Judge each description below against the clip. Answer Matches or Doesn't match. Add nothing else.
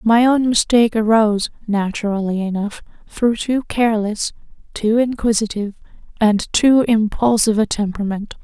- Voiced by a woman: Matches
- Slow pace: Matches